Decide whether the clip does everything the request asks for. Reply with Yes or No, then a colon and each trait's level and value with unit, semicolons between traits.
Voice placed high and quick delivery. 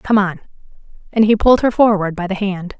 Yes: high, 200 Hz; fast, 215 wpm